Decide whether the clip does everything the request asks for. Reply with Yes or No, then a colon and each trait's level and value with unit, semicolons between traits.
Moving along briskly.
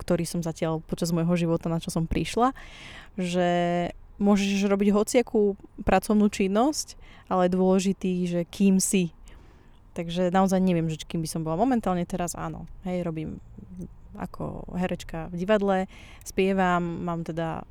No: average, 140 wpm